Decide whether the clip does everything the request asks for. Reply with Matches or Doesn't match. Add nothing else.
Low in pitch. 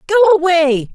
Doesn't match